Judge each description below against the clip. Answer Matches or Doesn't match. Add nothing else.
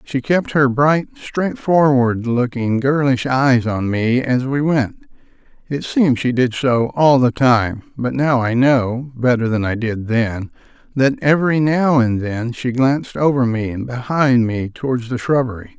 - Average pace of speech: Matches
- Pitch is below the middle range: Matches